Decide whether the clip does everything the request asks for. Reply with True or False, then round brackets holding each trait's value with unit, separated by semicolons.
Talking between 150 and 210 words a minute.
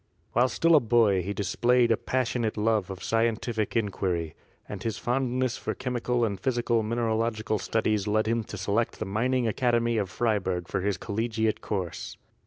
True (175 wpm)